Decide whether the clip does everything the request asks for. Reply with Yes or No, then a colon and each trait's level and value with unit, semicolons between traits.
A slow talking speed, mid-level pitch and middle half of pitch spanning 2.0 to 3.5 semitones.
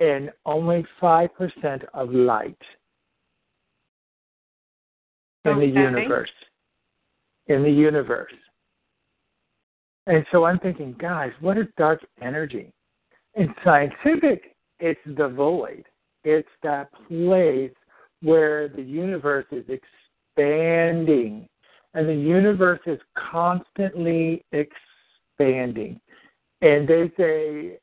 Yes: slow, 90 wpm; medium, 155 Hz; average, 3.0 semitones